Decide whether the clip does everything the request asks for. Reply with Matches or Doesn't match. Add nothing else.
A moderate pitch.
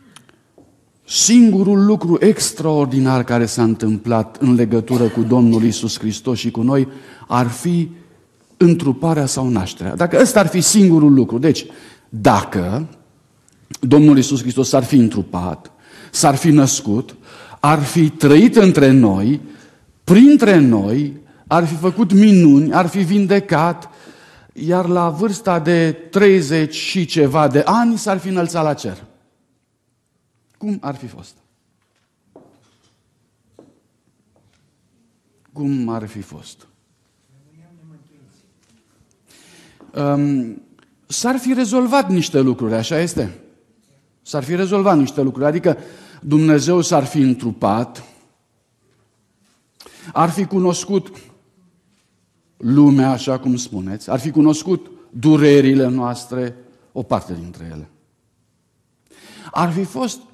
Matches